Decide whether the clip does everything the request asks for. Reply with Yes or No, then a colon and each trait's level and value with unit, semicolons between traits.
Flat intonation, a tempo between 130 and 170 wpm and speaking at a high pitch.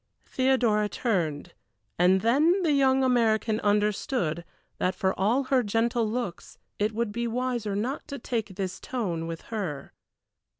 No: average, 4.7 semitones; average, 140 wpm; high, 220 Hz